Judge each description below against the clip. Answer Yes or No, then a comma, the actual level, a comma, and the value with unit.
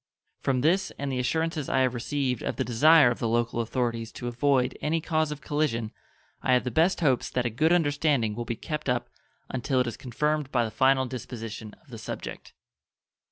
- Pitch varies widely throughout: No, average, 4.1 semitones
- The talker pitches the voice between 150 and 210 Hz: No, low, 130 Hz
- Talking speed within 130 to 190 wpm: No, fast, 205 wpm